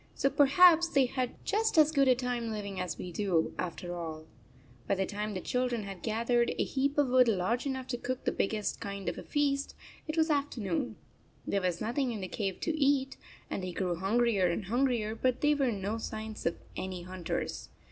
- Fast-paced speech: Yes, fast, 210 wpm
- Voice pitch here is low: No, high, 230 Hz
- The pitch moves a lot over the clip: Yes, wide, 5.8 semitones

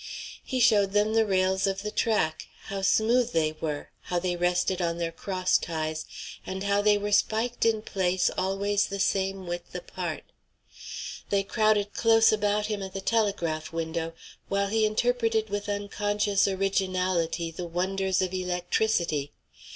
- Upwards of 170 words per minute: No, average, 150 wpm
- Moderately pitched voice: No, high, 195 Hz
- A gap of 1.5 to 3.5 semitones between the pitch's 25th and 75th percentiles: Yes, average, 2.8 semitones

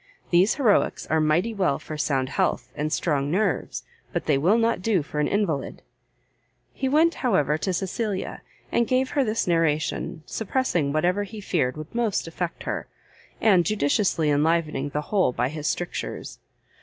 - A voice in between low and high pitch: Yes, medium, 175 Hz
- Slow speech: No, average, 160 wpm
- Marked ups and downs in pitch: Yes, wide, 6.0 semitones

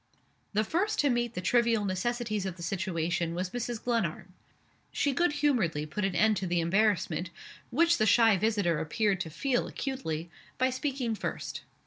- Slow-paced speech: No, average, 165 wpm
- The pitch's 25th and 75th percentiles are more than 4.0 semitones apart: Yes, wide, 5.5 semitones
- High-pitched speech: Yes, high, 215 Hz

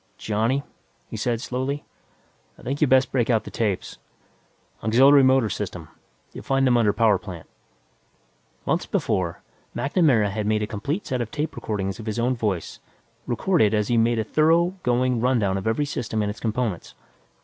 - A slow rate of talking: No, average, 170 wpm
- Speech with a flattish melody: No, average, 3.8 semitones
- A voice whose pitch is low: Yes, low, 115 Hz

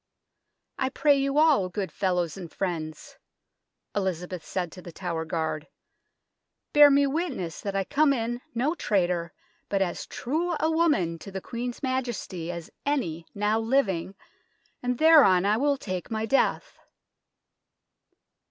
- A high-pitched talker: Yes, high, 205 Hz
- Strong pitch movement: Yes, wide, 7.6 semitones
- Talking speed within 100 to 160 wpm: Yes, average, 145 wpm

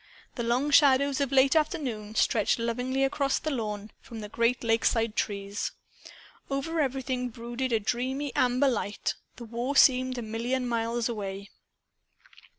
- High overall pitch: Yes, high, 245 Hz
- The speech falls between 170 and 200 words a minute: No, average, 145 wpm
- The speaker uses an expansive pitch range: No, average, 2.9 semitones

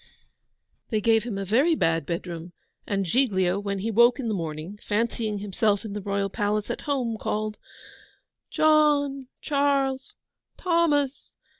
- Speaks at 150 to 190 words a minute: No, average, 140 wpm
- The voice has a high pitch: Yes, high, 215 Hz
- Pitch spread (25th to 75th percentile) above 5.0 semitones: Yes, wide, 5.4 semitones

